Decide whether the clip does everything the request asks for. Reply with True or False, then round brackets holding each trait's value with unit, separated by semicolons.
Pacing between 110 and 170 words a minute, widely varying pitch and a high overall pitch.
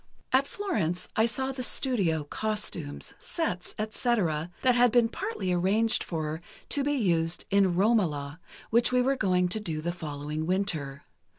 True (155 wpm; 6.7 semitones; 195 Hz)